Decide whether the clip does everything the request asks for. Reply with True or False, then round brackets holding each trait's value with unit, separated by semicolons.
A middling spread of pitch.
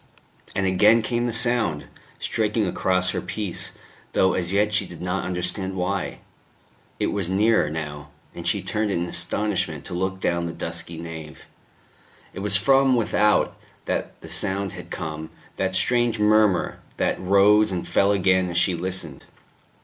True (3.3 semitones)